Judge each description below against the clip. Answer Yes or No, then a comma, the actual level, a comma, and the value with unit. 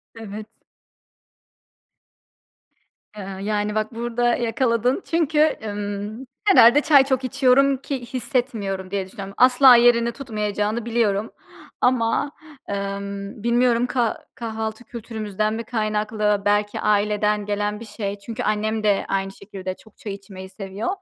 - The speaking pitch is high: Yes, high, 220 Hz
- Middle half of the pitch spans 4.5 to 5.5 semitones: No, average, 2.9 semitones